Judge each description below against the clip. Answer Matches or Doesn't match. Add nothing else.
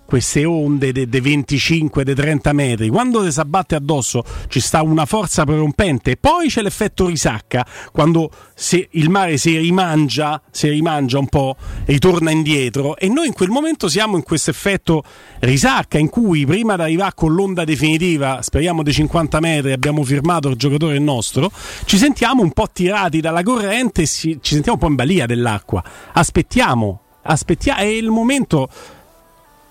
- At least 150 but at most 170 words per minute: Matches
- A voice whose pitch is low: Doesn't match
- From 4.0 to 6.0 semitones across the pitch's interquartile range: Matches